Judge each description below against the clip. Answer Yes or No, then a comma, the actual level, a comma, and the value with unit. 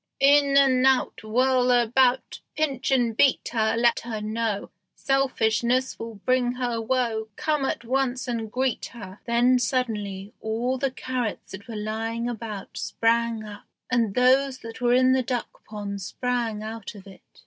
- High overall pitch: Yes, high, 235 Hz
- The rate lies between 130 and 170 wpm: Yes, average, 160 wpm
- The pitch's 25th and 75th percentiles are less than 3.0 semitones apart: Yes, narrow, 2.6 semitones